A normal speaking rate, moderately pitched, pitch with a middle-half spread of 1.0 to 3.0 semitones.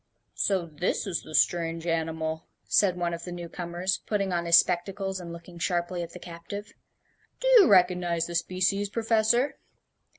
Yes: average, 165 wpm; medium, 175 Hz; narrow, 2.6 semitones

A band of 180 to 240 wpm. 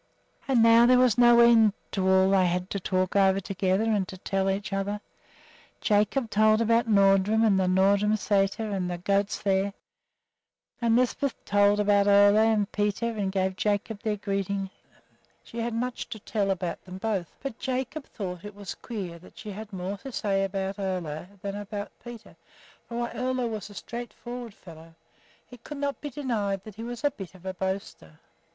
Yes: average, 185 wpm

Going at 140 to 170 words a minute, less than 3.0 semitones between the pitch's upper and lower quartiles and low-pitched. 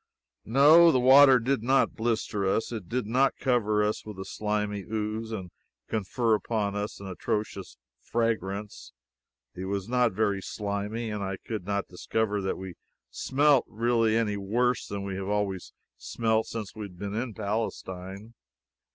Yes: average, 160 wpm; narrow, 2.6 semitones; low, 105 Hz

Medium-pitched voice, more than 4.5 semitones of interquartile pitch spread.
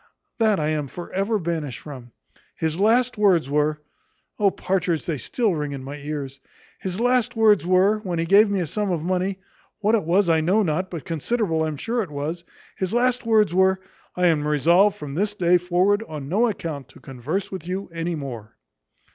Yes: medium, 180 Hz; average, 5.0 semitones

